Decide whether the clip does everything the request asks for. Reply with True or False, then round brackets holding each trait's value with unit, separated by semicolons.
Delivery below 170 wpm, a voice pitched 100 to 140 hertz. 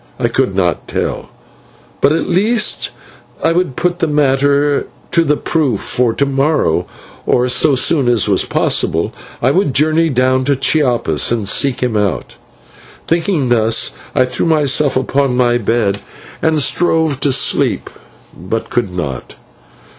True (145 wpm; 135 Hz)